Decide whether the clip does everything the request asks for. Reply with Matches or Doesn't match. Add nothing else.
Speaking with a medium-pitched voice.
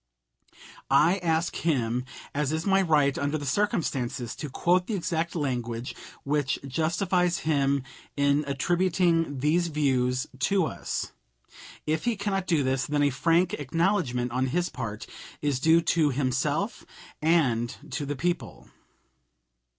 Matches